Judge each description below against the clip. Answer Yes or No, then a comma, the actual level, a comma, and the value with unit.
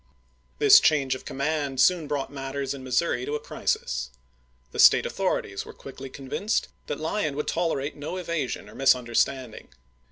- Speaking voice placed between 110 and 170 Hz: Yes, medium, 140 Hz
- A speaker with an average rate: Yes, average, 155 wpm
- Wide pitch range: No, average, 2.9 semitones